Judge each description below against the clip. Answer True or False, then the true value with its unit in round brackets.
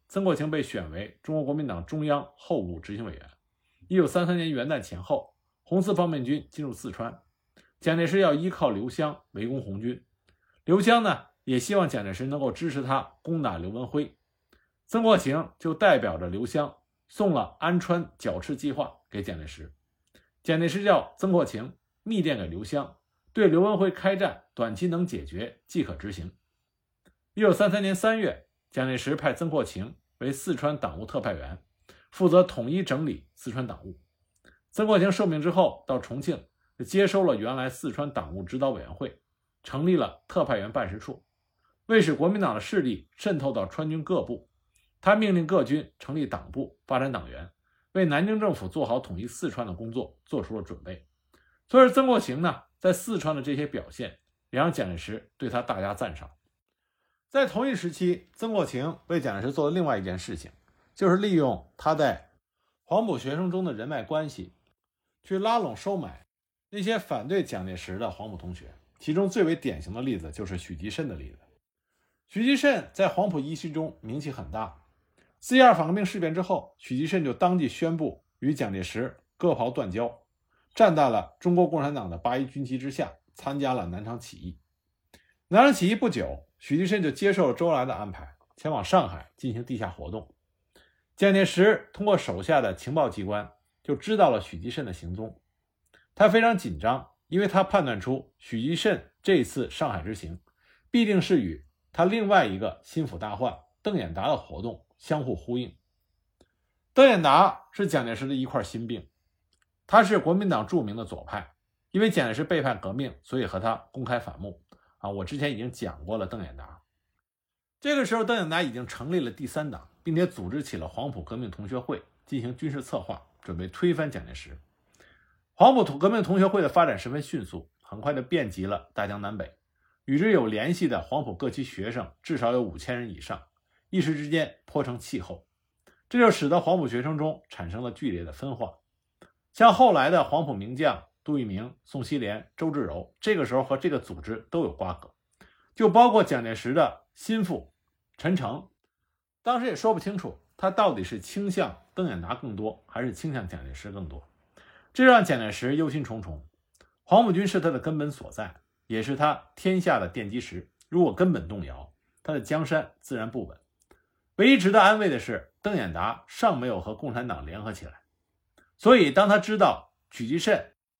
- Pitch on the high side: False (135 Hz)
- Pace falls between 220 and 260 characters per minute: False (275 characters per minute)